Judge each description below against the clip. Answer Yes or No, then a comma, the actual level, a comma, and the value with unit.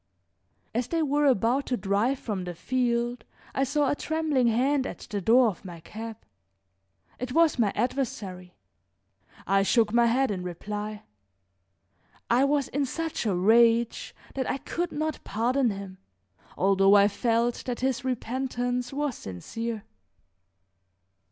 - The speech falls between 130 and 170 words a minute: Yes, average, 140 wpm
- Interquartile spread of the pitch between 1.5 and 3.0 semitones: No, average, 4.4 semitones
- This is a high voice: Yes, high, 235 Hz